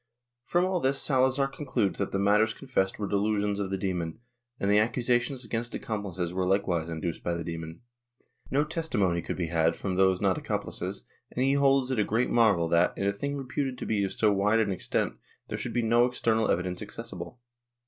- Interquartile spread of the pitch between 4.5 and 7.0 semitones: Yes, average, 5.1 semitones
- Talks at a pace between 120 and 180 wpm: No, average, 200 wpm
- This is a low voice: Yes, low, 105 Hz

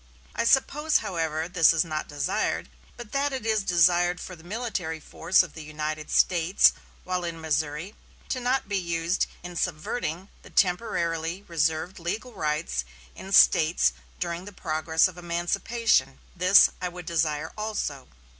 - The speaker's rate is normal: Yes, average, 150 wpm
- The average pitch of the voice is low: No, medium, 175 Hz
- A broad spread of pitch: No, average, 3.3 semitones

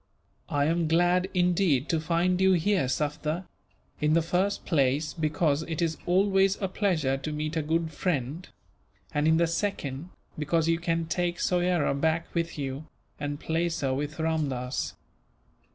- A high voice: No, medium, 160 Hz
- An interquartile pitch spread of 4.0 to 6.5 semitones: No, average, 2.9 semitones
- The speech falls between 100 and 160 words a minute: Yes, average, 155 wpm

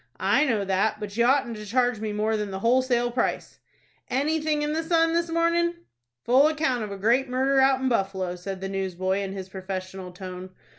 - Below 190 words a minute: No, average, 200 wpm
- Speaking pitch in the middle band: No, high, 230 Hz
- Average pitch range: No, wide, 5.9 semitones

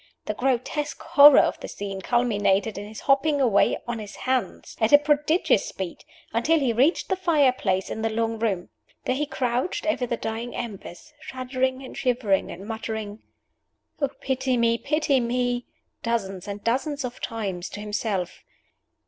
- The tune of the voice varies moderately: Yes, average, 4.1 semitones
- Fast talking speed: No, average, 165 wpm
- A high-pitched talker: Yes, high, 240 Hz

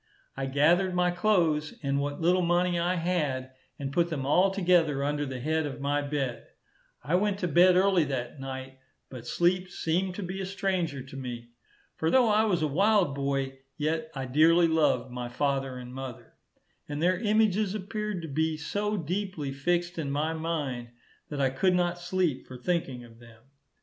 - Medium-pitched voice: Yes, medium, 160 Hz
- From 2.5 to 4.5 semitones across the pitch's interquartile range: No, average, 4.9 semitones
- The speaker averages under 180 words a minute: No, average, 185 wpm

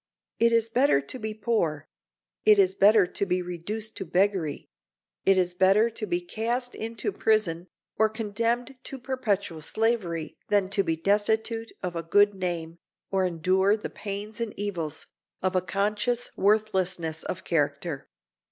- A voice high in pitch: Yes, high, 200 Hz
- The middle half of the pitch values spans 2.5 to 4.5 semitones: Yes, average, 3.8 semitones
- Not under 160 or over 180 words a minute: No, average, 150 wpm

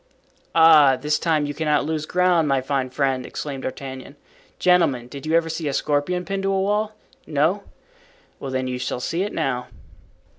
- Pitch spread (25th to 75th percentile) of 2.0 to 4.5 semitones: Yes, average, 3.9 semitones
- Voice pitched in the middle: Yes, medium, 150 Hz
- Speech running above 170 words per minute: Yes, average, 180 wpm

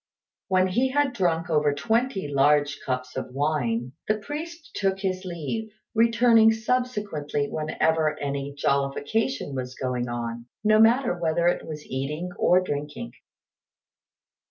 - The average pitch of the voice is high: No, medium, 165 Hz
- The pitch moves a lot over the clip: Yes, wide, 7.7 semitones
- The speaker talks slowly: Yes, slow, 130 wpm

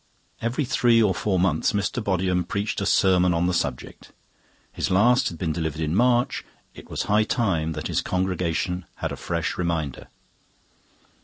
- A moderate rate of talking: Yes, average, 165 wpm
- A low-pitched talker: Yes, very low, 90 Hz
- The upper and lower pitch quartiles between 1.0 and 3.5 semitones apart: No, average, 3.9 semitones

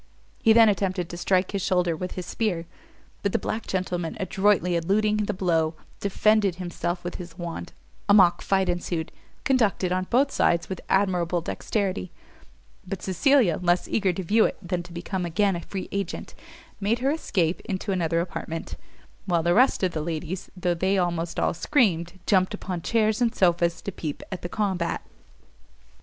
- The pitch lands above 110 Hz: Yes, medium, 185 Hz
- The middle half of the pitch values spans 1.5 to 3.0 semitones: Yes, average, 2.7 semitones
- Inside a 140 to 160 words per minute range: No, average, 175 wpm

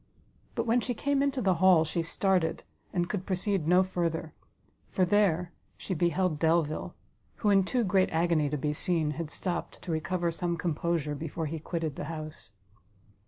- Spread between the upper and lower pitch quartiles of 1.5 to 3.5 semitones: Yes, average, 2.9 semitones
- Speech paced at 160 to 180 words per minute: Yes, average, 170 wpm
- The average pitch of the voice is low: No, medium, 170 Hz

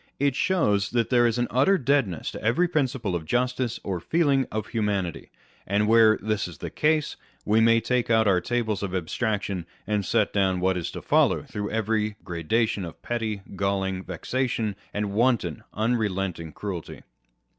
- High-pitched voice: No, low, 110 Hz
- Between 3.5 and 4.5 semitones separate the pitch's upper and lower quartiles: Yes, average, 3.9 semitones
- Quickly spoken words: No, average, 170 wpm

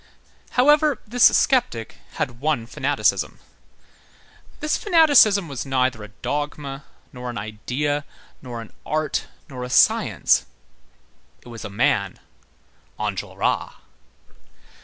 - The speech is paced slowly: Yes, slow, 105 wpm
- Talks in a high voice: No, low, 135 Hz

